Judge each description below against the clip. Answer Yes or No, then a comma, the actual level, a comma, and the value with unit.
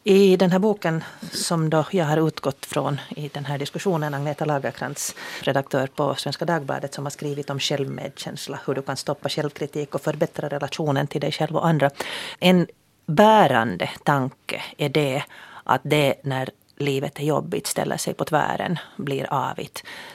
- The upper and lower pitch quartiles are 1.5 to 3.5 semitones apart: Yes, average, 2.9 semitones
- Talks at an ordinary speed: No, fast, 165 wpm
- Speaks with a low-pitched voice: No, medium, 150 Hz